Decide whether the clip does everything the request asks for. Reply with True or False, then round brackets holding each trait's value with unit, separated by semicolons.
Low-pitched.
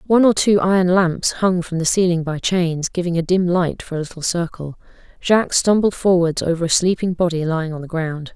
False (175 Hz)